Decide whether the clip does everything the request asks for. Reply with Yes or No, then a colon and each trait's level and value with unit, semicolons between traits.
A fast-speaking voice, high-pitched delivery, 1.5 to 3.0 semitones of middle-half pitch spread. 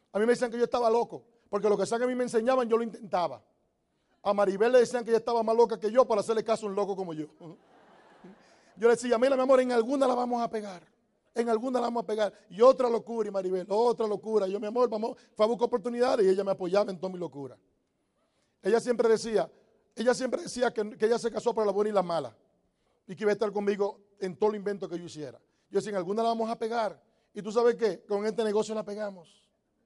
Yes: fast, 255 wpm; high, 220 Hz; narrow, 2.6 semitones